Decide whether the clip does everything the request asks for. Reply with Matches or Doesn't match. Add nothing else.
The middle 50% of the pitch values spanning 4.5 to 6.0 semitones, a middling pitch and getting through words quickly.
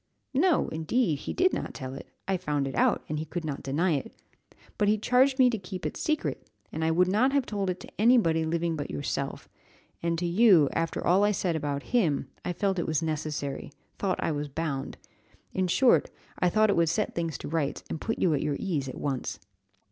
Matches